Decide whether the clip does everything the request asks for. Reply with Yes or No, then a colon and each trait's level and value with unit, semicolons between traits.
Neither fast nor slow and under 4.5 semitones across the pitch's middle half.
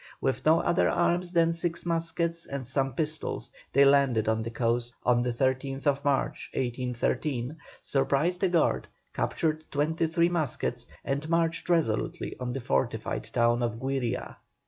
No: average, 145 wpm; average, 5.1 semitones